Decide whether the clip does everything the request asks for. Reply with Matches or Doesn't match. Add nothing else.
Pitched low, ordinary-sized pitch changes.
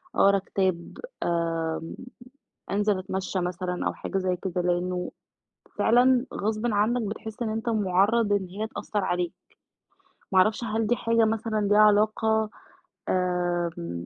Doesn't match